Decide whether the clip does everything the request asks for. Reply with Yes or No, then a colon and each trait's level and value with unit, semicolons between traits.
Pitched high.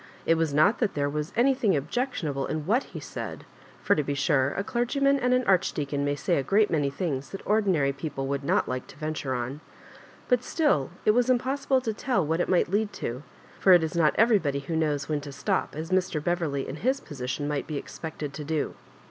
No: medium, 160 Hz